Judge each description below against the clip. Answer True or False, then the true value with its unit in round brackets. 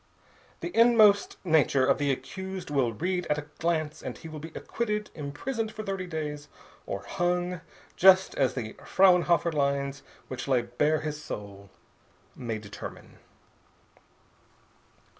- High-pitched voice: False (155 Hz)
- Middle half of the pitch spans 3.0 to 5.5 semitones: True (5.1 semitones)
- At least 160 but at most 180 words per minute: False (140 wpm)